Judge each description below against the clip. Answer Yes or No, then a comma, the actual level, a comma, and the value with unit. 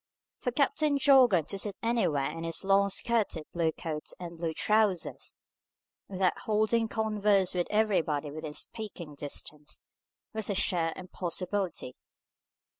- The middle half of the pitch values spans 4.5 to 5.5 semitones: Yes, average, 4.9 semitones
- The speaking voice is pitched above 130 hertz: Yes, high, 190 Hz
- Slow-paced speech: Yes, slow, 125 wpm